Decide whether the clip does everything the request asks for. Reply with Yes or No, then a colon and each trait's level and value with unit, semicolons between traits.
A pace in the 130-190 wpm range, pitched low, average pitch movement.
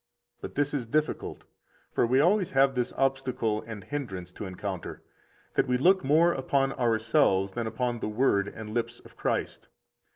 Yes: average, 170 wpm; low, 125 Hz; average, 4.2 semitones